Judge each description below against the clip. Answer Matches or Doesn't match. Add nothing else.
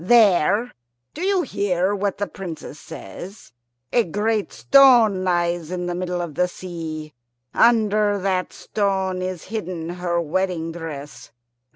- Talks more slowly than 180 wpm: Matches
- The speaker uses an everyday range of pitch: Matches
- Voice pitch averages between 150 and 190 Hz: Matches